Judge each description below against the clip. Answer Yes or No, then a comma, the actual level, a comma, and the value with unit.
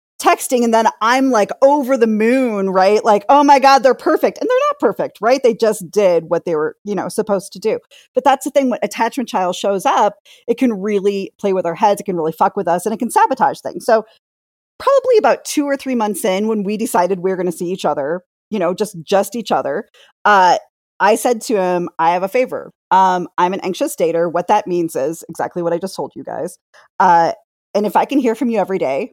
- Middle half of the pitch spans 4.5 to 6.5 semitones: Yes, average, 5.3 semitones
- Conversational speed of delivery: No, fast, 240 wpm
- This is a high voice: Yes, high, 210 Hz